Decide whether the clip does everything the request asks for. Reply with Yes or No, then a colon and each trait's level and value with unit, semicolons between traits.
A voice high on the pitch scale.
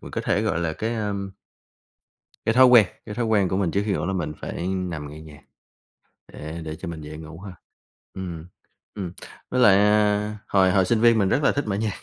No: very low, 95 Hz